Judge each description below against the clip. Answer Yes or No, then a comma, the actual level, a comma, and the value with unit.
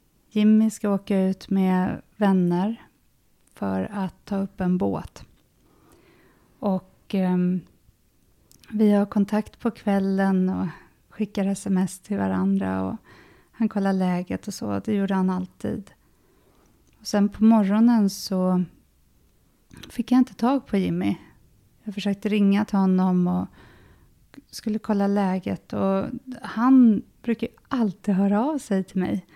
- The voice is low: No, high, 195 Hz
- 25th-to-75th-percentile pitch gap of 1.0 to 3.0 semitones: Yes, narrow, 2.6 semitones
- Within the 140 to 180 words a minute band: No, average, 130 wpm